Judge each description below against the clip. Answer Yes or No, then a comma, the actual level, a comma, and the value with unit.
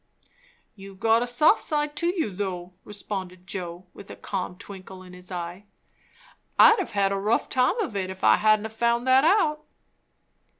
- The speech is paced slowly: No, average, 170 wpm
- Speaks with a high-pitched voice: Yes, high, 205 Hz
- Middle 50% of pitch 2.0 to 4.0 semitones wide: No, average, 5.2 semitones